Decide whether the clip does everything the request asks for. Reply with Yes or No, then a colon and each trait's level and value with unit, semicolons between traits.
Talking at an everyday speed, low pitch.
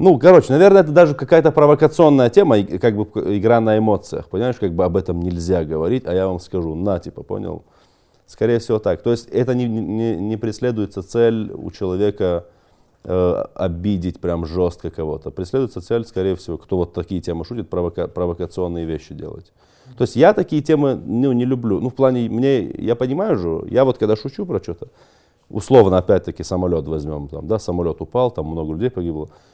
No: fast, 185 wpm; low, 105 Hz